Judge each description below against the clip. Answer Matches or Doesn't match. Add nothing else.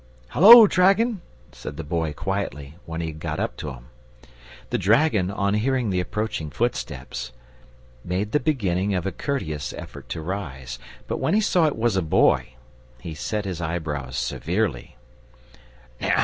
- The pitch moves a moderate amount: Doesn't match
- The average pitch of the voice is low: Matches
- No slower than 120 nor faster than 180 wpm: Matches